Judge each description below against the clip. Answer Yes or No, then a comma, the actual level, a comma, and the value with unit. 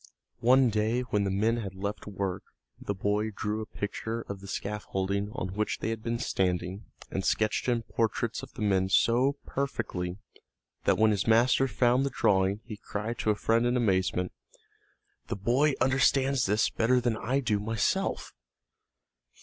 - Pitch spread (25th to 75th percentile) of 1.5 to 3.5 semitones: Yes, average, 3.1 semitones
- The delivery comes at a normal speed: Yes, average, 165 wpm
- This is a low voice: Yes, low, 110 Hz